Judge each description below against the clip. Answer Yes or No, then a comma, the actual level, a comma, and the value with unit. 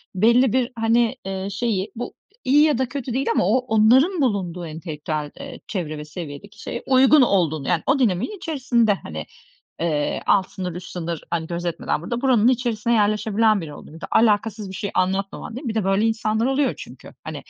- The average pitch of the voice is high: Yes, high, 215 Hz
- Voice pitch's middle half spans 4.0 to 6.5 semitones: Yes, wide, 5.6 semitones